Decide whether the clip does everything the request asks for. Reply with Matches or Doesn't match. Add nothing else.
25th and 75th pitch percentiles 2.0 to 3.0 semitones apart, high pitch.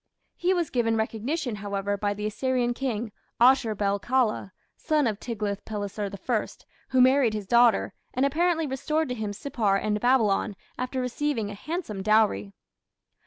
Doesn't match